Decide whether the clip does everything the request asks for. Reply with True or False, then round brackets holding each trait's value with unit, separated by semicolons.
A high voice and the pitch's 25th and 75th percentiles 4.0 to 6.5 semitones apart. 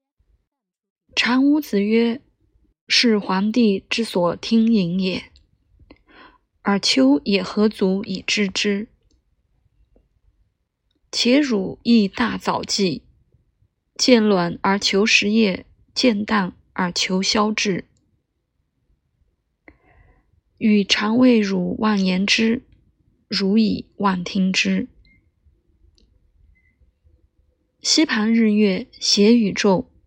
False (205 Hz; 3.3 semitones)